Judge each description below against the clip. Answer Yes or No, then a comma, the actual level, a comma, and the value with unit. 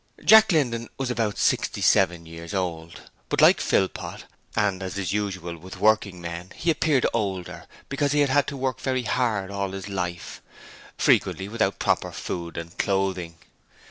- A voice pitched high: No, low, 100 Hz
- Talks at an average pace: Yes, average, 165 wpm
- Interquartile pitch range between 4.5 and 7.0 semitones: Yes, wide, 5.6 semitones